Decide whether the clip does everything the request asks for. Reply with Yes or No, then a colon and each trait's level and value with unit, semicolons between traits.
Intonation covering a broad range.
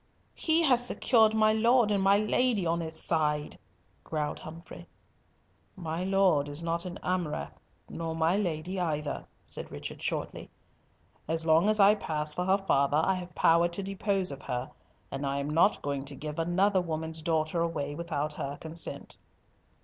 No: average, 4.1 semitones